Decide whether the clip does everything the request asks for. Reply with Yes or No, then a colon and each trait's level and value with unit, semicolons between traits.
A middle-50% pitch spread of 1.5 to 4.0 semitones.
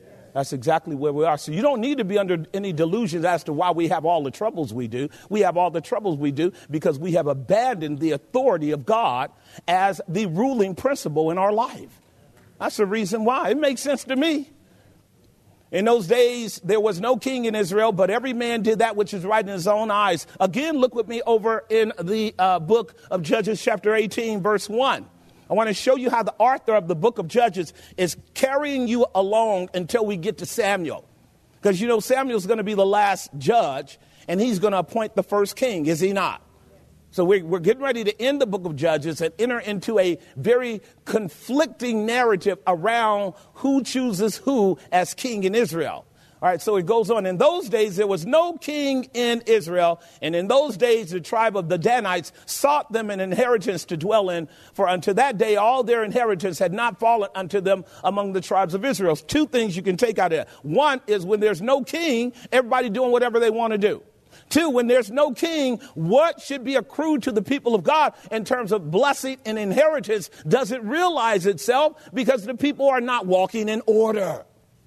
No: average, 4.8 semitones